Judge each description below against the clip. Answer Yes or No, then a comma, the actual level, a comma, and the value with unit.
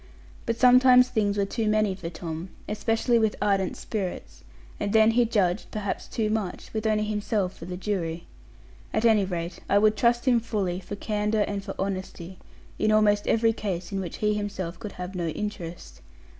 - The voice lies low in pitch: No, high, 205 Hz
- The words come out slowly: No, average, 185 wpm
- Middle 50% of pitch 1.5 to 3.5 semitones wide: Yes, average, 2.8 semitones